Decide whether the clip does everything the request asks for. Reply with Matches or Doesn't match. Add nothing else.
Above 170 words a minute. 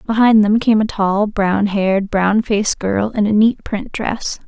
Matches